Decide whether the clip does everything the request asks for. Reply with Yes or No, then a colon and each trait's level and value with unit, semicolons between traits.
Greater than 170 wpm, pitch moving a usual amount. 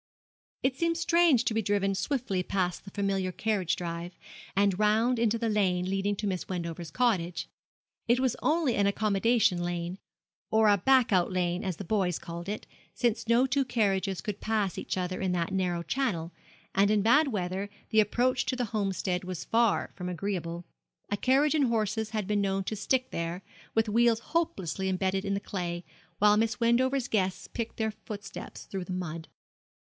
Yes: average, 180 wpm; average, 4.0 semitones